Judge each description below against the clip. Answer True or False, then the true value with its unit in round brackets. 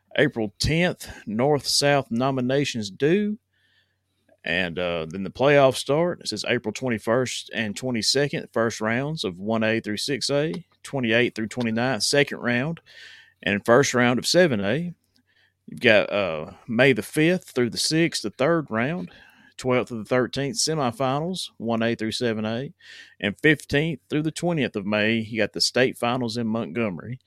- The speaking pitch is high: False (125 Hz)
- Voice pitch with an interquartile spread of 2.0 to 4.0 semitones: False (4.7 semitones)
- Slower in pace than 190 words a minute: True (150 wpm)